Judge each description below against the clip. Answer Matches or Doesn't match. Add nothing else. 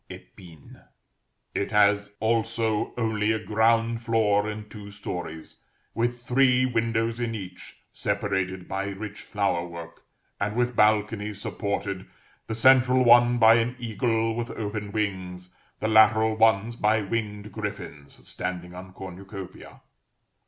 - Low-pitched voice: Matches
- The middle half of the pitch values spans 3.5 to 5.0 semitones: Doesn't match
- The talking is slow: Matches